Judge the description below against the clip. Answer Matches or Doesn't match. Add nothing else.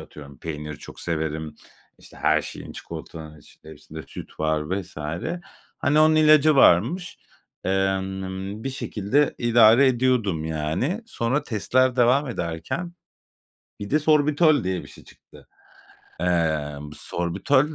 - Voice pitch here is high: Doesn't match